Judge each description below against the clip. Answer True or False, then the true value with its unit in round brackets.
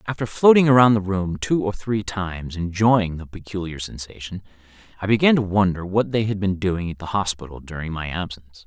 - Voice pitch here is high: False (95 Hz)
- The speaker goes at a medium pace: True (195 wpm)